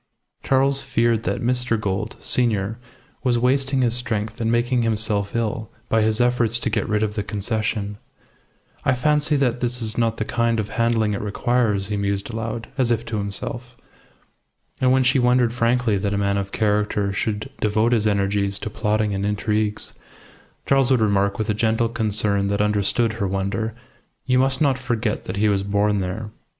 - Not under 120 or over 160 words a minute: No, average, 180 wpm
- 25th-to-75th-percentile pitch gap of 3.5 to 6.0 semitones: No, average, 2.7 semitones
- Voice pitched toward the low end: Yes, low, 110 Hz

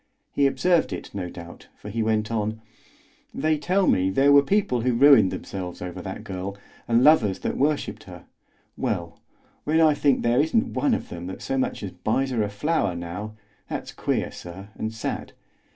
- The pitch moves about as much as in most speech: No, wide, 7.0 semitones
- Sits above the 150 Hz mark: No, low, 115 Hz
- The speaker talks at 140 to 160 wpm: No, average, 185 wpm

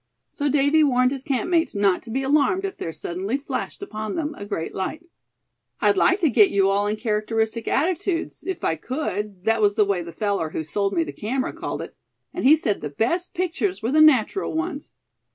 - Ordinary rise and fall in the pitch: No, wide, 7.6 semitones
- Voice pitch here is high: Yes, very high, 250 Hz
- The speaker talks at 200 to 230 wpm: Yes, fast, 205 wpm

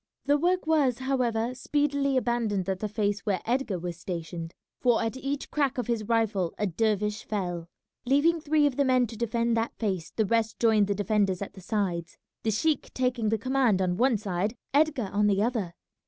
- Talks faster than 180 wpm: Yes, average, 195 wpm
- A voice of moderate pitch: No, high, 225 Hz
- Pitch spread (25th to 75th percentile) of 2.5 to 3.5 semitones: No, average, 4.6 semitones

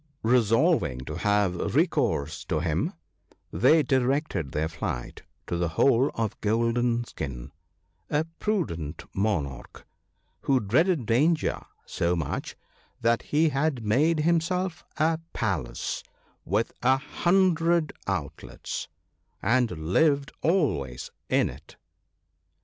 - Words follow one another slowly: Yes, slow, 110 wpm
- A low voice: Yes, low, 115 Hz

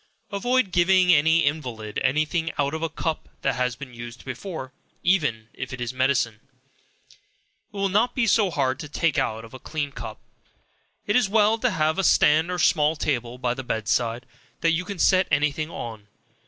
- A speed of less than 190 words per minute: No, average, 195 wpm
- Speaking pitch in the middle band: Yes, medium, 150 Hz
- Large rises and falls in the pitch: Yes, wide, 6.3 semitones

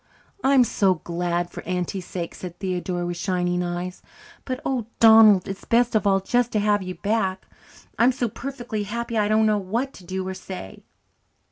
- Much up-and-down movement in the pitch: No, average, 4.0 semitones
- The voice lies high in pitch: Yes, high, 195 Hz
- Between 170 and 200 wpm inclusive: Yes, average, 190 wpm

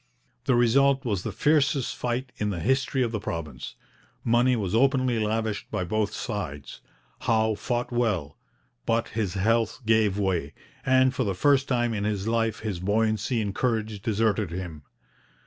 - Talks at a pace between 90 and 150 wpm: No, average, 160 wpm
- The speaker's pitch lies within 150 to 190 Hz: No, low, 110 Hz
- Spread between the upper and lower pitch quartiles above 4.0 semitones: No, average, 3.2 semitones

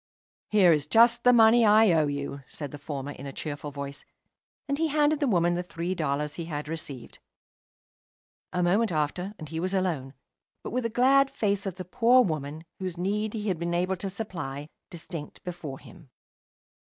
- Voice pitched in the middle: Yes, medium, 175 Hz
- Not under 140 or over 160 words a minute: No, average, 190 wpm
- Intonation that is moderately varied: No, wide, 6.3 semitones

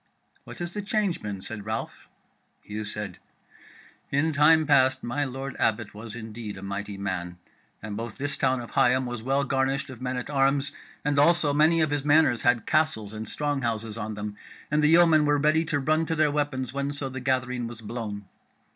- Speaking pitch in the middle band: No, low, 130 Hz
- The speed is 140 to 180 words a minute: No, average, 195 wpm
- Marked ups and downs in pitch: No, average, 4.9 semitones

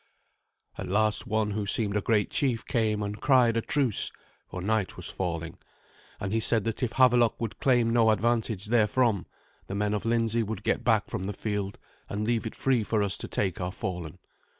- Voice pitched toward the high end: No, low, 110 Hz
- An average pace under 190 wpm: No, average, 195 wpm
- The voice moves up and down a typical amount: No, narrow, 2.3 semitones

